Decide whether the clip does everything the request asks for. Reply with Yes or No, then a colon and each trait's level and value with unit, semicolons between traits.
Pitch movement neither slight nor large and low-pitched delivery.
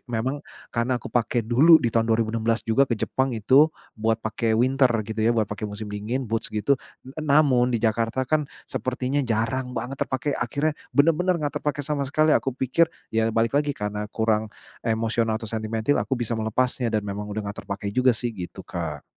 Yes: average, 3.3 semitones; low, 115 Hz